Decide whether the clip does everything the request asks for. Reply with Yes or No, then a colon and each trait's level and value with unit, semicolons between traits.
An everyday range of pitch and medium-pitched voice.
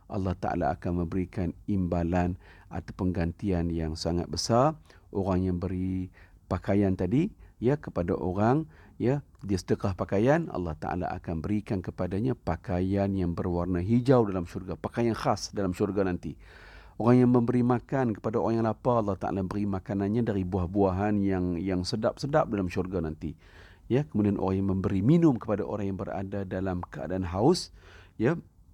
No: average, 3.4 semitones; very low, 95 Hz